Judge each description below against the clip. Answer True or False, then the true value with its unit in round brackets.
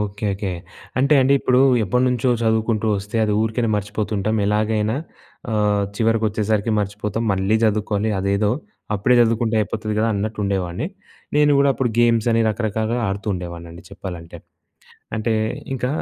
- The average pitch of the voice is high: False (110 Hz)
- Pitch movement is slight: True (2.1 semitones)